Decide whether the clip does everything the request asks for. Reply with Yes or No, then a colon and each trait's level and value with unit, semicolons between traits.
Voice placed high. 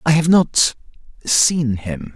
No: low, 130 Hz